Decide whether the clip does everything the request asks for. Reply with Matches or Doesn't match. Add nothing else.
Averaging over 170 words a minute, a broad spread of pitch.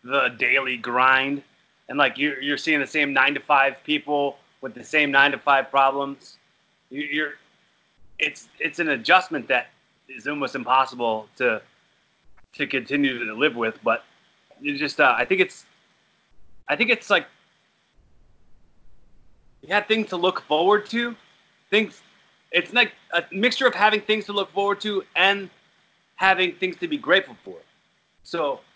Doesn't match